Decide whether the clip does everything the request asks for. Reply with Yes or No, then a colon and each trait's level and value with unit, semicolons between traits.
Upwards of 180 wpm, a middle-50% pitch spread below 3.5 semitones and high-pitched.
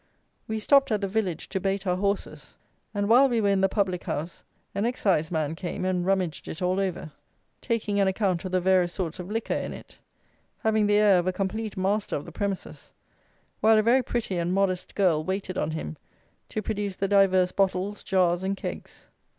Yes: average, 200 wpm; narrow, 2.4 semitones; high, 195 Hz